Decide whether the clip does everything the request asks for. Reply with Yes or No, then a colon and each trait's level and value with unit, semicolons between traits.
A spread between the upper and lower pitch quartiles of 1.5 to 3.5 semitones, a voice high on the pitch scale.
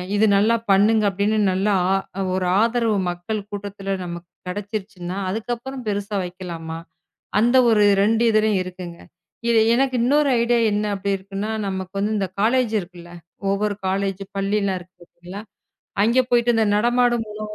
Yes: average, 3.0 semitones; high, 205 Hz